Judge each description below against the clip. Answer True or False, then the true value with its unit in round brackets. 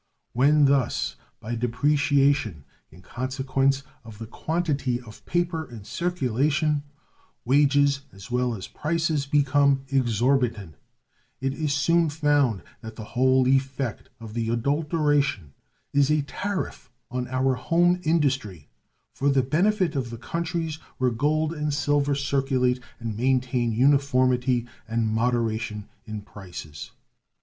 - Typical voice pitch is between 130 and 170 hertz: True (135 Hz)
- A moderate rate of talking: False (125 wpm)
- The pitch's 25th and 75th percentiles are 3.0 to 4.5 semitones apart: True (3.7 semitones)